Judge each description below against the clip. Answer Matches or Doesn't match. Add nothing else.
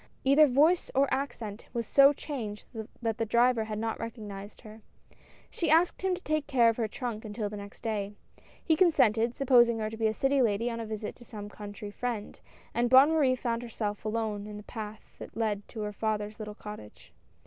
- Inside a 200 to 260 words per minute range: Matches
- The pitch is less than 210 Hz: Doesn't match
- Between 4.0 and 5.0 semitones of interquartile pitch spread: Doesn't match